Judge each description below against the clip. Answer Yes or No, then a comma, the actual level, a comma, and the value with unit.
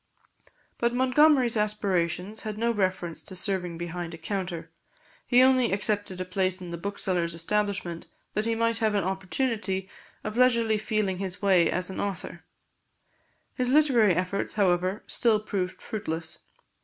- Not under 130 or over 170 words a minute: Yes, average, 145 wpm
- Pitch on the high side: Yes, high, 200 Hz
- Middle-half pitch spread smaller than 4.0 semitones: Yes, average, 3.4 semitones